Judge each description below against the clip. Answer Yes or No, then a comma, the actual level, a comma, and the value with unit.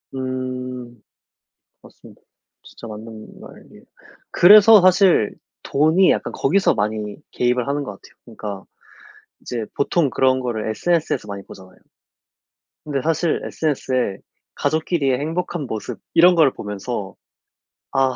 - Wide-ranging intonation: Yes, wide, 6.3 semitones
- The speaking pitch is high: No, low, 130 Hz